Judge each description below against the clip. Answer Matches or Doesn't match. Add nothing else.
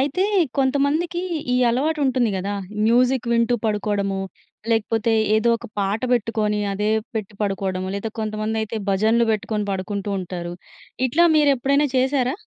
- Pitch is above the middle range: Matches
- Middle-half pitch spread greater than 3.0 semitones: Matches